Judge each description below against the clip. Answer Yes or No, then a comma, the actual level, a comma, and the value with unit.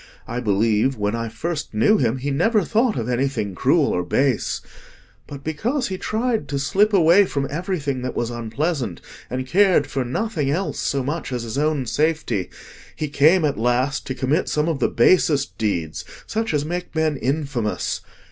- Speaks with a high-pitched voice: No, medium, 140 Hz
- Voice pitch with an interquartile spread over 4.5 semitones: Yes, wide, 5.5 semitones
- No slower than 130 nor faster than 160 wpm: No, average, 175 wpm